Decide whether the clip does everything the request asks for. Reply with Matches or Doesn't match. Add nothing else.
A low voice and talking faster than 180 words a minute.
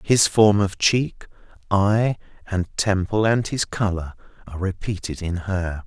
Doesn't match